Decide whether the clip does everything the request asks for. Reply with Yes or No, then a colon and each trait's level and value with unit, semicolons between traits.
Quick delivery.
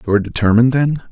Yes: fast, 215 wpm